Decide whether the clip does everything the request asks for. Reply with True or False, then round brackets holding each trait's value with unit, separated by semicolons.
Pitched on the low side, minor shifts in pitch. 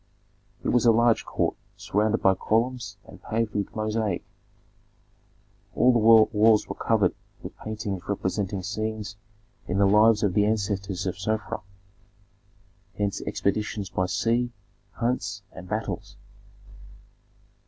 True (105 Hz; 2.1 semitones)